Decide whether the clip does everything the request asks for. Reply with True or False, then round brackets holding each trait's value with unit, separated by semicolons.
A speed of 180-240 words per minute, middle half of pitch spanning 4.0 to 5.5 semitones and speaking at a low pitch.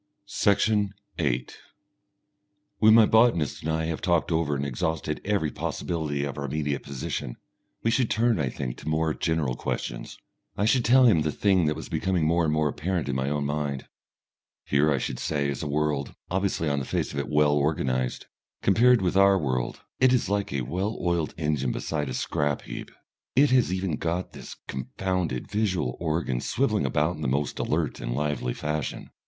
True (185 wpm; 4.9 semitones; 75 Hz)